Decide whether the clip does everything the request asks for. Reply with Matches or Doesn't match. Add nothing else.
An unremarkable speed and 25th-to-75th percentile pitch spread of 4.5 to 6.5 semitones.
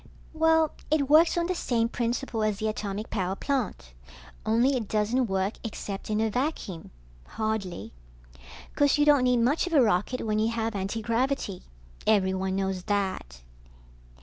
Matches